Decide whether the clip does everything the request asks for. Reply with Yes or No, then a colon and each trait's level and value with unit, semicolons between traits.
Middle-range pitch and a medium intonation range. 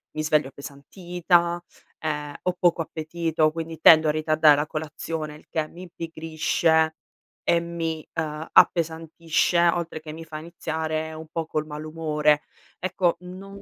No: medium, 160 Hz; narrow, 1.6 semitones